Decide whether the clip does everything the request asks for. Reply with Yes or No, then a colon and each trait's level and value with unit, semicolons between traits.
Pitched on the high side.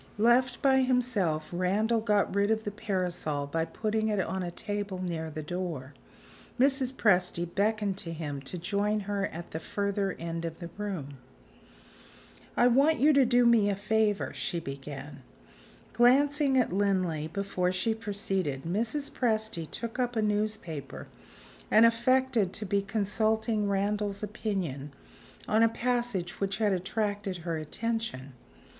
Yes: high, 205 Hz